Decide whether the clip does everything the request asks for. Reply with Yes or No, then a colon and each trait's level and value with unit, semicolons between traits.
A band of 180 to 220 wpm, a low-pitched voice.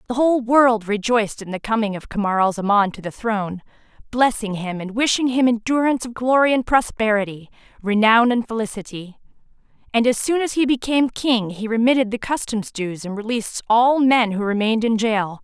No: average, 185 wpm; high, 225 Hz